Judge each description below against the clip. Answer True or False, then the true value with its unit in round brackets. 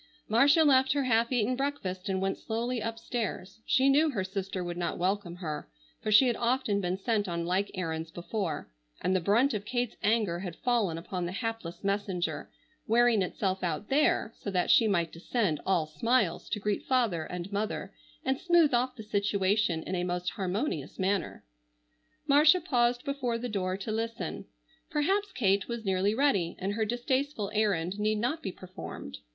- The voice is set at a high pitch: True (210 Hz)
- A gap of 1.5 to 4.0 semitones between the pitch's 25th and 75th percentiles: False (4.8 semitones)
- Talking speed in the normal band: True (175 wpm)